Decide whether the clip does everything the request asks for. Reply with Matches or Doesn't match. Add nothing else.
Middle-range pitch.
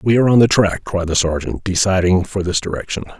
Doesn't match